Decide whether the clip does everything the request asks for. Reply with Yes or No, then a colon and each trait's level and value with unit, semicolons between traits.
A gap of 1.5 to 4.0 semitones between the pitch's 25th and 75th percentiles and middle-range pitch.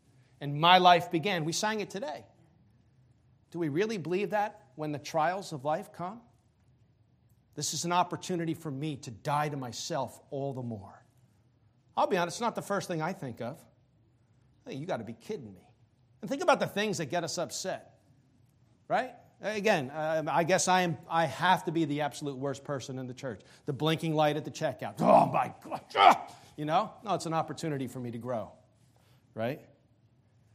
No: wide, 5.5 semitones; medium, 145 Hz